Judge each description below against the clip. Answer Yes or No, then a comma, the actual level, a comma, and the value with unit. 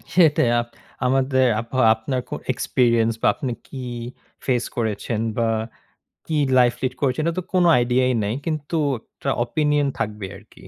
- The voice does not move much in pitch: No, average, 3.5 semitones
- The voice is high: No, low, 130 Hz